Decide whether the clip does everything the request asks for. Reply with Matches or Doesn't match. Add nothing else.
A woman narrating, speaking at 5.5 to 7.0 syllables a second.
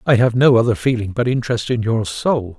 Doesn't match